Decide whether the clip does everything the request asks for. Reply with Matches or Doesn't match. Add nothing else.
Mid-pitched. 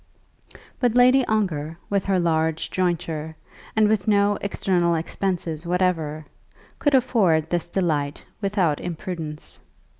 Matches